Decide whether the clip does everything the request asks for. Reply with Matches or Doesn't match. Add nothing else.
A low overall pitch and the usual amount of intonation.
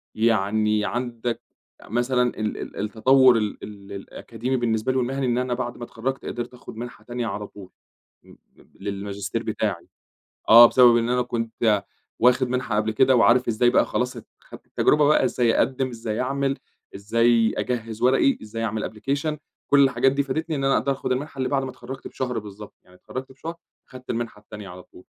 Matches